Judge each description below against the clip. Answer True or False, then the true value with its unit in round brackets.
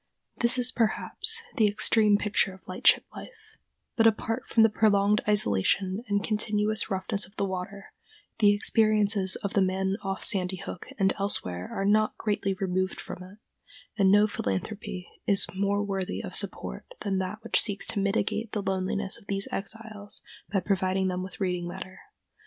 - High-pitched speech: True (200 Hz)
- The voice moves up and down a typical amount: False (2.0 semitones)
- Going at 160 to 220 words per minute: True (165 wpm)